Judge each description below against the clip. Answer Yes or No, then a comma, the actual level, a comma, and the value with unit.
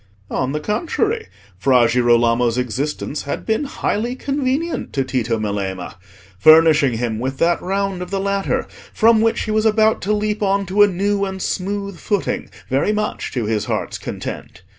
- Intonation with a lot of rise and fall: Yes, wide, 8.9 semitones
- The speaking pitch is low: No, medium, 185 Hz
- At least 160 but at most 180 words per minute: Yes, average, 165 wpm